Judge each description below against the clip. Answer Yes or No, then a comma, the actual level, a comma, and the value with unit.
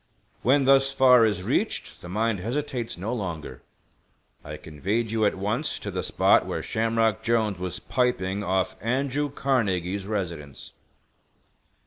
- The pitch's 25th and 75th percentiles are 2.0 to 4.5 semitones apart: No, average, 5.1 semitones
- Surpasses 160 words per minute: No, slow, 135 wpm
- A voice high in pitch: No, low, 110 Hz